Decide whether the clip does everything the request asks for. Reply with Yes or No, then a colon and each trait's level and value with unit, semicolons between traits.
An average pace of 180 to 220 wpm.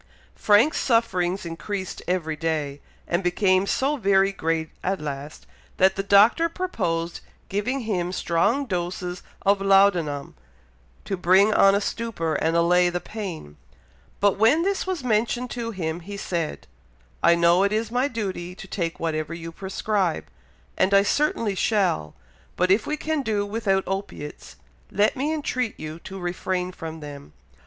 No: average, 155 wpm